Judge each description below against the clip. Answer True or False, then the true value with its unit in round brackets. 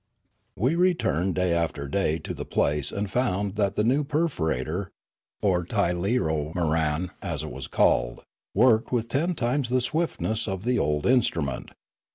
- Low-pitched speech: True (95 Hz)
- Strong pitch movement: True (7.5 semitones)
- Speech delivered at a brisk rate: False (155 wpm)